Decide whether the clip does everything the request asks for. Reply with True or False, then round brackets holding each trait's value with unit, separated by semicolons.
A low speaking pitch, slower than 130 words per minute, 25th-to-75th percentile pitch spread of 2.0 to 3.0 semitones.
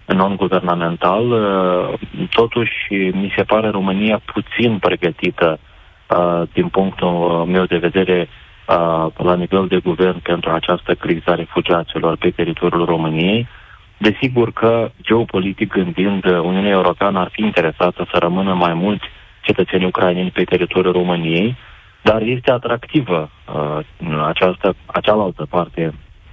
True (90 Hz; 115 wpm; 2.4 semitones)